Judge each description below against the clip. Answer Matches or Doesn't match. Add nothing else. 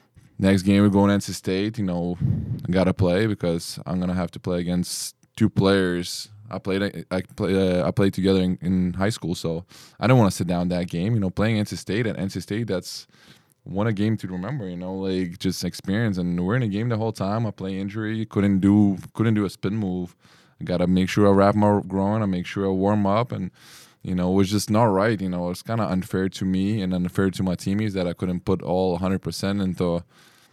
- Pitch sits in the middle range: Doesn't match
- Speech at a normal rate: Doesn't match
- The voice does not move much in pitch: Matches